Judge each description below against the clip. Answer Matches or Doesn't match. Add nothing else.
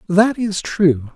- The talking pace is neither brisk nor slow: Matches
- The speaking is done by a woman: Doesn't match